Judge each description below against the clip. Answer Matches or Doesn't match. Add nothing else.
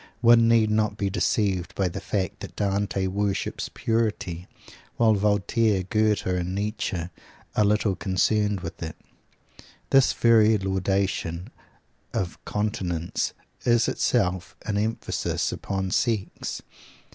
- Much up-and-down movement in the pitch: Doesn't match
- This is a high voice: Doesn't match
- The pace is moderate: Doesn't match